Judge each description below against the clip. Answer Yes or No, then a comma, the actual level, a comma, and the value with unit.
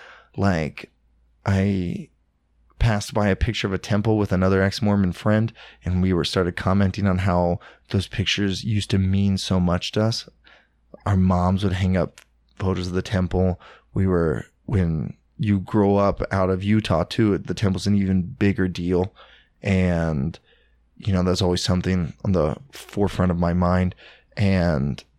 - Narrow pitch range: Yes, narrow, 1.9 semitones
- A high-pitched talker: No, very low, 95 Hz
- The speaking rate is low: No, average, 160 wpm